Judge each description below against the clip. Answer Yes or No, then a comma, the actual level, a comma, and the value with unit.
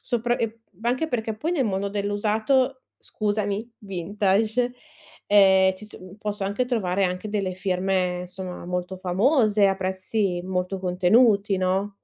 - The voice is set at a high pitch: Yes, high, 200 Hz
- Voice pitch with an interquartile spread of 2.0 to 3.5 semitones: Yes, average, 2.7 semitones